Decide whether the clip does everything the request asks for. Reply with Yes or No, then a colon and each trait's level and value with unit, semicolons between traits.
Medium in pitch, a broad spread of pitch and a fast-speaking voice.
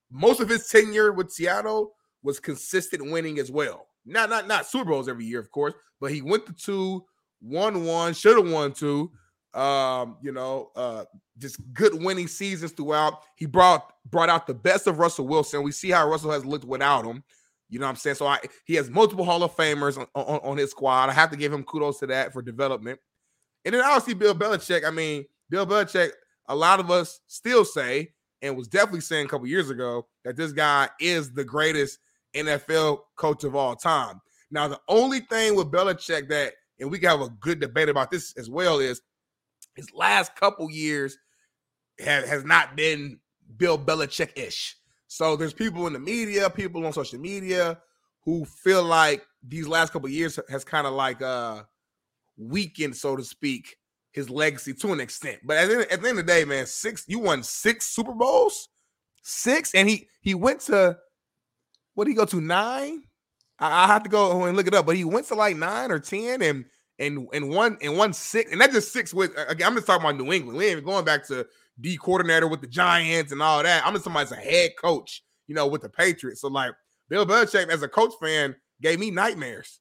Yes: medium, 165 Hz; wide, 5.8 semitones; fast, 210 wpm